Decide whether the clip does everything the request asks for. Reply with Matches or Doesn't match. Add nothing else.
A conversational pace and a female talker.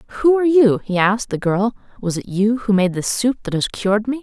Doesn't match